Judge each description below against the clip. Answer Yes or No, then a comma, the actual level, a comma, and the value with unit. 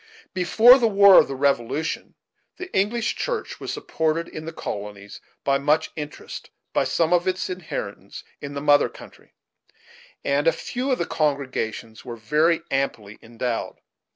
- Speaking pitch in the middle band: Yes, medium, 155 Hz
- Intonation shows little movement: No, average, 5.3 semitones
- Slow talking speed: No, average, 155 wpm